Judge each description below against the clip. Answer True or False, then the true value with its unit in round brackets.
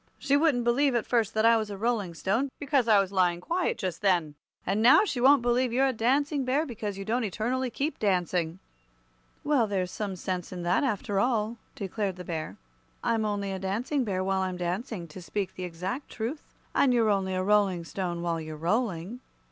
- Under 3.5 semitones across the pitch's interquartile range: False (4.8 semitones)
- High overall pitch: True (210 Hz)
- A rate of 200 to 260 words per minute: True (205 wpm)